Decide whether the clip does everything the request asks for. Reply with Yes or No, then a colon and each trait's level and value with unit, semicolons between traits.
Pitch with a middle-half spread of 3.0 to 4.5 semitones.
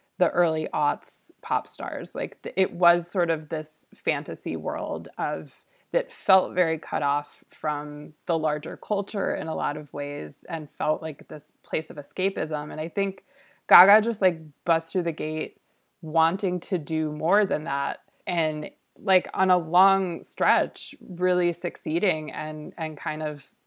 Yes: average, 3.6 semitones